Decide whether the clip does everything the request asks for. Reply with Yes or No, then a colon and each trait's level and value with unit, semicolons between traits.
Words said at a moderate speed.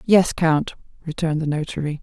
Yes: average, 150 wpm